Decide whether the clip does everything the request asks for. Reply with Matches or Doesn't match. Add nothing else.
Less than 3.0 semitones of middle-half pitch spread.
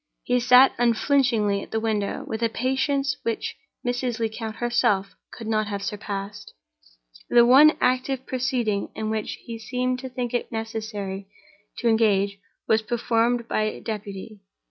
Matches